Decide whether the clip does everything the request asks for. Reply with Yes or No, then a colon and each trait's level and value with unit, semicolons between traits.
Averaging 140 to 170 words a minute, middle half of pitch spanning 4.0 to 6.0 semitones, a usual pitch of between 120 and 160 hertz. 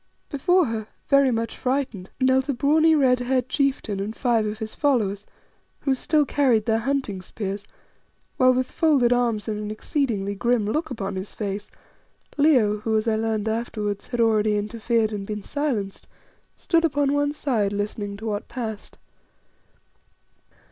No: average, 155 wpm; average, 4.5 semitones; high, 230 Hz